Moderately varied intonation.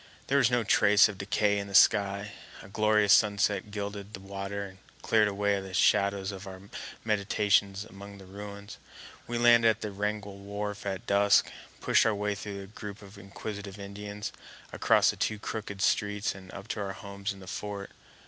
No: narrow, 1.0 semitones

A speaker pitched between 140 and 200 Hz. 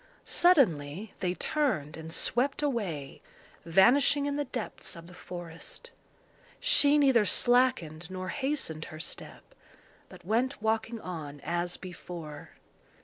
Yes: high, 190 Hz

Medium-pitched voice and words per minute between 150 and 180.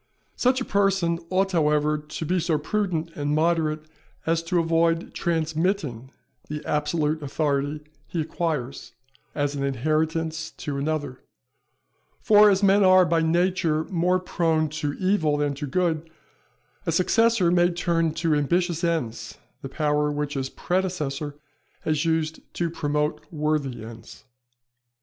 No: medium, 160 Hz; slow, 135 wpm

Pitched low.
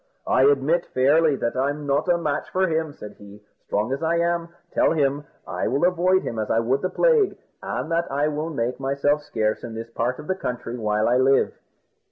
No: medium, 145 Hz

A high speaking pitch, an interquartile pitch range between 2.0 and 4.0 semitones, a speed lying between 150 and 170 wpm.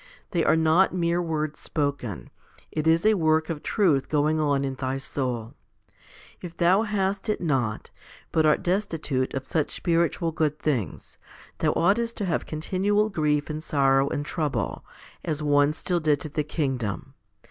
No: medium, 155 Hz; average, 3.2 semitones; average, 160 wpm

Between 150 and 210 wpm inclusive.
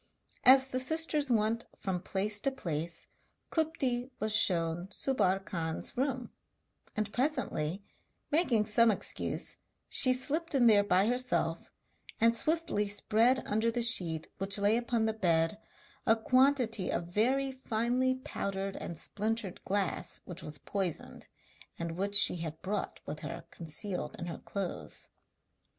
No: slow, 135 wpm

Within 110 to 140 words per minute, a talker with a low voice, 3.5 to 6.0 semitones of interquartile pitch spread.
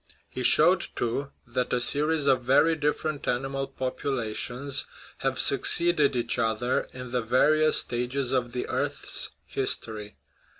No: slow, 135 wpm; low, 130 Hz; narrow, 2.6 semitones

